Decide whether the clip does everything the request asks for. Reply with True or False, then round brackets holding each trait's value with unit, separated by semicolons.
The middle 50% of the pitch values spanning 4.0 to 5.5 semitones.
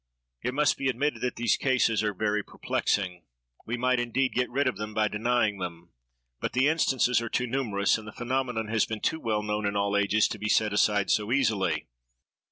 False (3.3 semitones)